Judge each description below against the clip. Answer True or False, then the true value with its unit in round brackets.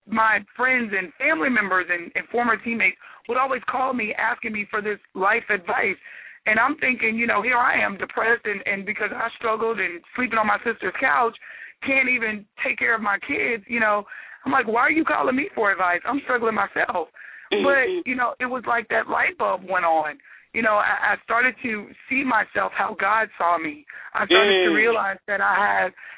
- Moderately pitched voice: False (225 Hz)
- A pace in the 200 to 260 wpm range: True (205 wpm)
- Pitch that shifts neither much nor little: True (3.6 semitones)